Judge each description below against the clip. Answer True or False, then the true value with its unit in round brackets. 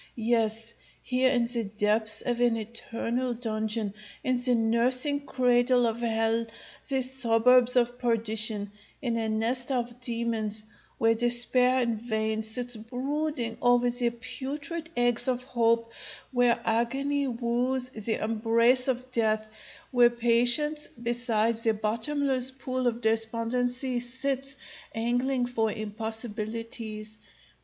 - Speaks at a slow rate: True (120 wpm)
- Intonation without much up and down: True (1.9 semitones)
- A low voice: False (235 Hz)